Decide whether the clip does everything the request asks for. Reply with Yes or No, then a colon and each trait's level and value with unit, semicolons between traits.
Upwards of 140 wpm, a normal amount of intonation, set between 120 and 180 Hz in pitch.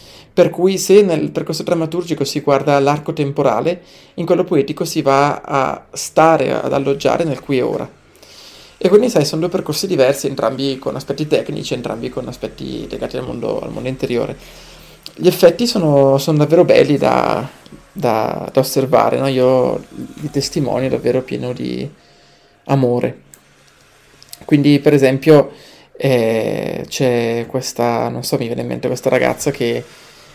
Yes: average, 150 wpm; average, 4.3 semitones; medium, 140 Hz